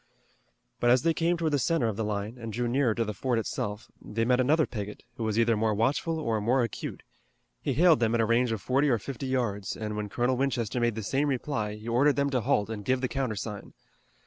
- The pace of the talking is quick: Yes, fast, 240 wpm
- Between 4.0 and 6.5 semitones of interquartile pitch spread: No, average, 3.6 semitones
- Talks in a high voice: No, low, 120 Hz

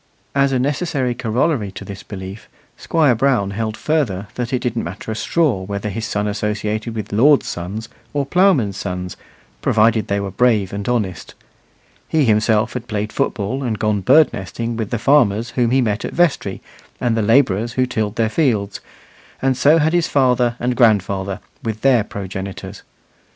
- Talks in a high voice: No, low, 110 Hz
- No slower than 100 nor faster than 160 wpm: No, average, 170 wpm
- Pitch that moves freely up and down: No, average, 4.2 semitones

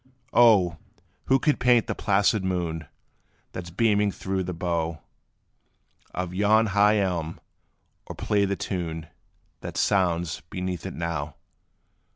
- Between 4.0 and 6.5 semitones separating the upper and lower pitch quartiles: No, average, 3.4 semitones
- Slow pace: Yes, slow, 130 wpm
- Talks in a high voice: No, very low, 95 Hz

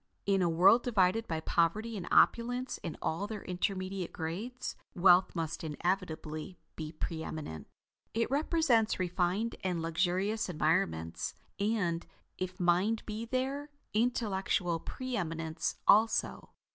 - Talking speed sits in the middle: No, slow, 120 wpm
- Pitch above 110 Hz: Yes, medium, 185 Hz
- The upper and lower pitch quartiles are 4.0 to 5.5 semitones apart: Yes, average, 5.1 semitones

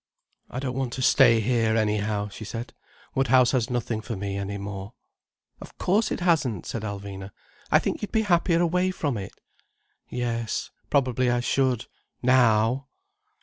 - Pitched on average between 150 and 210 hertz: No, low, 120 Hz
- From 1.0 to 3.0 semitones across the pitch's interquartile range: No, average, 3.9 semitones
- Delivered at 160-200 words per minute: No, average, 150 wpm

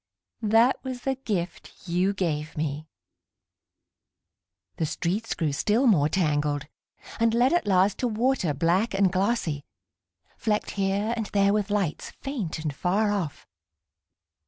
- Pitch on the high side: Yes, high, 195 Hz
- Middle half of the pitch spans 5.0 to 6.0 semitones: Yes, wide, 5.5 semitones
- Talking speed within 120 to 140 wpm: Yes, slow, 135 wpm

